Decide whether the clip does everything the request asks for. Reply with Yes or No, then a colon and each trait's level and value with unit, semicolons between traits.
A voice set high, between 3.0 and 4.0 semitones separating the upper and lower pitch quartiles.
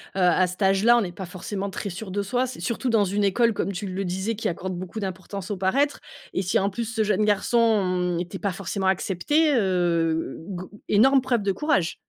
Yes: high, 195 Hz; average, 3.5 semitones